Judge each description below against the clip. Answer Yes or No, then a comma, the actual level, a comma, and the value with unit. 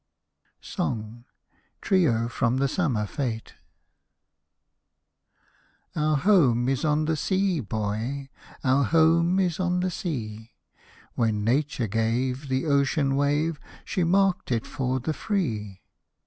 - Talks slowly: Yes, slow, 110 wpm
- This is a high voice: No, medium, 140 Hz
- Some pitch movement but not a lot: No, wide, 5.9 semitones